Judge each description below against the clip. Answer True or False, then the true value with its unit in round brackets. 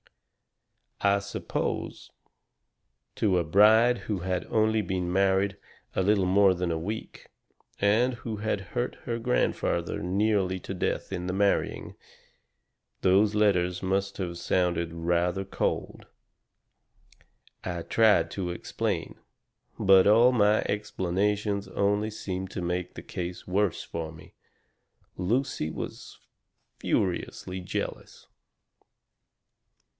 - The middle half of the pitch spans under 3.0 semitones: True (2.6 semitones)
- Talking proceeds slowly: True (110 wpm)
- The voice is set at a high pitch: False (95 Hz)